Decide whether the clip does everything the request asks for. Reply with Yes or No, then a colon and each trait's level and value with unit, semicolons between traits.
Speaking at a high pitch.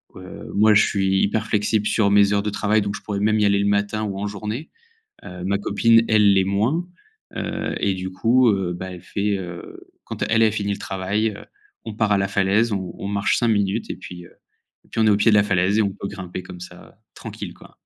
No: low, 100 Hz